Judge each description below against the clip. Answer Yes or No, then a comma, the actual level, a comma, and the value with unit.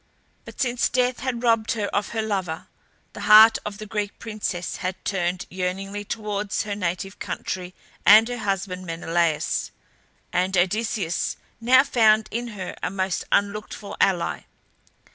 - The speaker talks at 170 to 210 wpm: No, average, 145 wpm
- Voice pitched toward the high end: Yes, high, 205 Hz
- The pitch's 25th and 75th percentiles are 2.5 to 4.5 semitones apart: Yes, average, 3.1 semitones